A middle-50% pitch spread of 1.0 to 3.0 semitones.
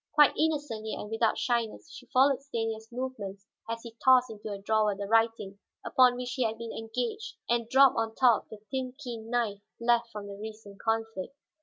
Yes: narrow, 2.5 semitones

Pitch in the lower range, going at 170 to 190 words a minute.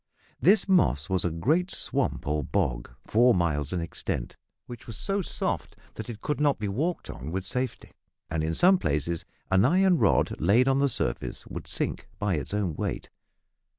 Yes: low, 105 Hz; average, 185 wpm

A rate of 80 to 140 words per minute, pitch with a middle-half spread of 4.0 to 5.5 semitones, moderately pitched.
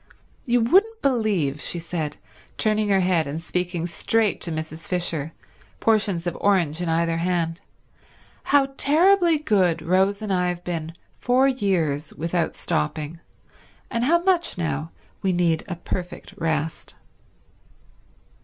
Yes: slow, 135 wpm; average, 4.9 semitones; medium, 180 Hz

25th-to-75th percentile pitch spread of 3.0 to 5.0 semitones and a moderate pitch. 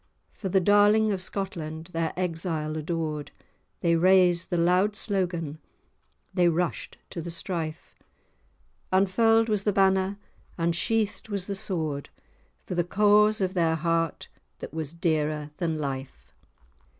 Yes: average, 3.3 semitones; medium, 175 Hz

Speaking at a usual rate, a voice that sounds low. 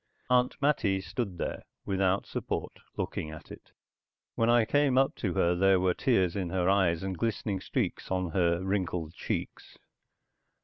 Yes: average, 160 wpm; very low, 95 Hz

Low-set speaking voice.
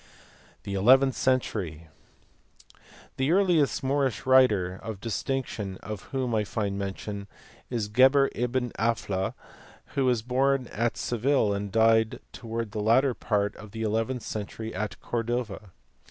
Yes: low, 115 Hz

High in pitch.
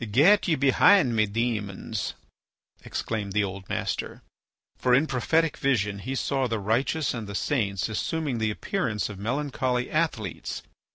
No: low, 120 Hz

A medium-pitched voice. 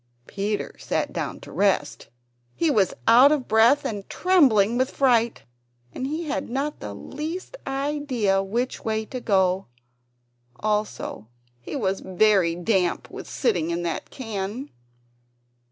No: high, 220 Hz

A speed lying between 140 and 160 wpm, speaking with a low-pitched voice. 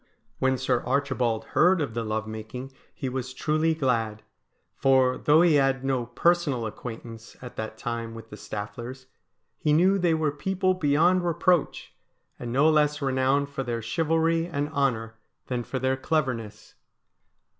Yes: average, 155 wpm; low, 130 Hz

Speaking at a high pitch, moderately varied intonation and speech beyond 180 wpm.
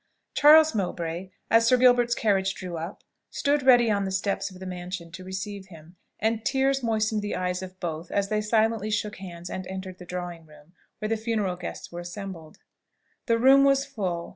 Yes: high, 195 Hz; average, 4.0 semitones; average, 190 wpm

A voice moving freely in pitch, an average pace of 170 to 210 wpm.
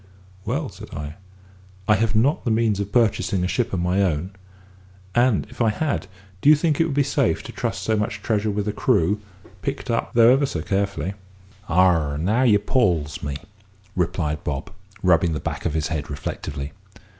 Yes: wide, 5.9 semitones; average, 190 wpm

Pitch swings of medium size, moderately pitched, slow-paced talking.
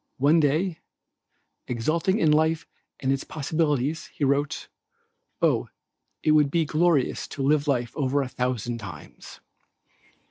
Yes: average, 3.2 semitones; medium, 145 Hz; slow, 130 wpm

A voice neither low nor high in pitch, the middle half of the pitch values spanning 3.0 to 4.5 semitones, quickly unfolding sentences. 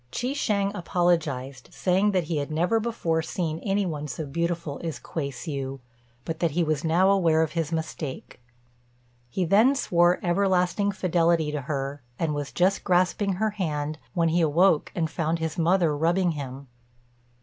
No: medium, 165 Hz; average, 3.3 semitones; average, 165 wpm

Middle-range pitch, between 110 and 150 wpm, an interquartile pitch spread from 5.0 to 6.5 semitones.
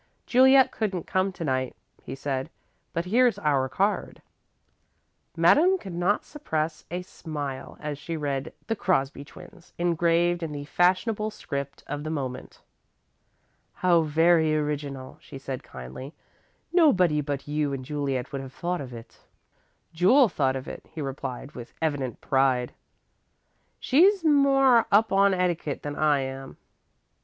Yes: medium, 155 Hz; average, 140 wpm; wide, 5.5 semitones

